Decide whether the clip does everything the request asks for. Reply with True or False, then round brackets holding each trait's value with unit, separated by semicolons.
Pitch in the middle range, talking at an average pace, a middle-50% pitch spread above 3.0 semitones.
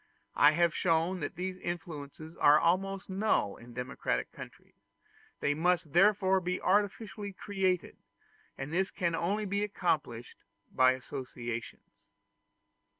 False (175 Hz; 120 wpm; 4.8 semitones)